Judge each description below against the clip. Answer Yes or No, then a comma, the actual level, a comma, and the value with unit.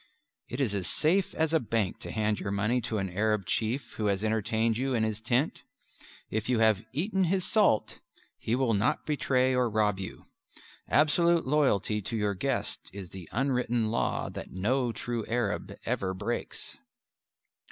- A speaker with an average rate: Yes, average, 170 wpm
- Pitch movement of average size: Yes, average, 3.8 semitones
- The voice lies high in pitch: No, low, 115 Hz